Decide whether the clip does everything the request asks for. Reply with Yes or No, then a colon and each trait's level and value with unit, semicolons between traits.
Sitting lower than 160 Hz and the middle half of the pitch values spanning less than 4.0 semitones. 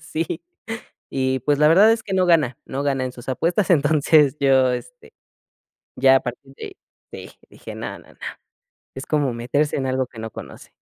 Yes: medium, 140 Hz; average, 3.4 semitones